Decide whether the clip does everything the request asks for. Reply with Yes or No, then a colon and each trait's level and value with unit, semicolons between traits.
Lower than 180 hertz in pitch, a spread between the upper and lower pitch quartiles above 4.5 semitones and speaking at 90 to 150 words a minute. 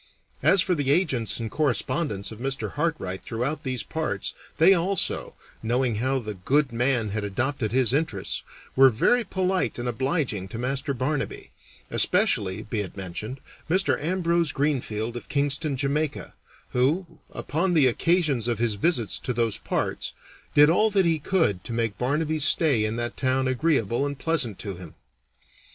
No: low, 135 Hz; wide, 5.5 semitones; average, 160 wpm